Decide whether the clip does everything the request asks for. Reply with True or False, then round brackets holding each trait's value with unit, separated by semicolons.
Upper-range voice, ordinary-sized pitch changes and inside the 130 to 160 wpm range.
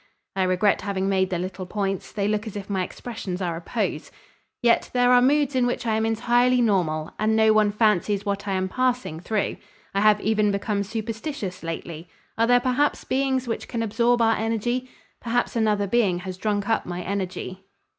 False (210 Hz; 3.7 semitones; 195 wpm)